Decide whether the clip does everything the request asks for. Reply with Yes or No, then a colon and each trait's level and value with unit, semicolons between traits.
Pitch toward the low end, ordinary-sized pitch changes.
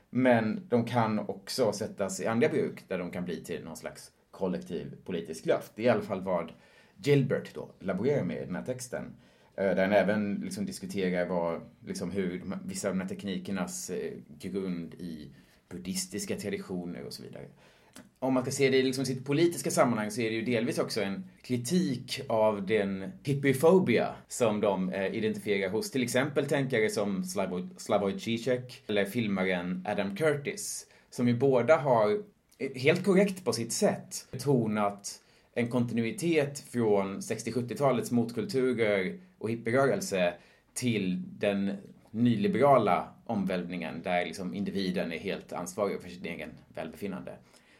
No: low, 115 Hz; wide, 5.7 semitones